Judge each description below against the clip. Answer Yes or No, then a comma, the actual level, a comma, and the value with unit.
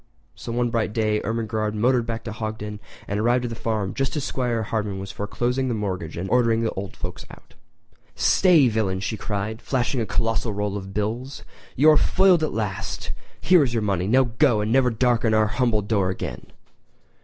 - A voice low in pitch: Yes, low, 110 Hz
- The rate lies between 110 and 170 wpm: No, average, 190 wpm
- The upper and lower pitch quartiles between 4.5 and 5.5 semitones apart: No, average, 2.8 semitones